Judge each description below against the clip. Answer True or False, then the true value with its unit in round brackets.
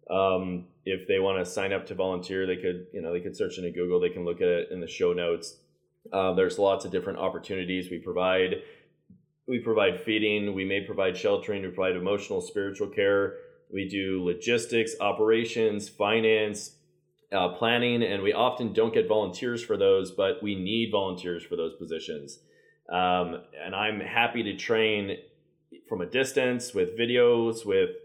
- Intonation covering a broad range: True (6.2 semitones)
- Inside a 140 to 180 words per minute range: True (175 wpm)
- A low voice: True (110 Hz)